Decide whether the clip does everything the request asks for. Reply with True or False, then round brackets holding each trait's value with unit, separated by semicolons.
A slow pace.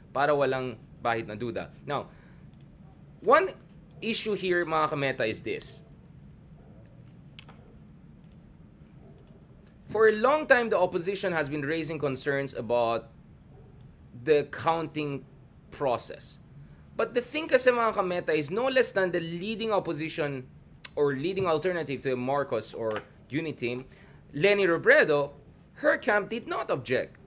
True (120 wpm)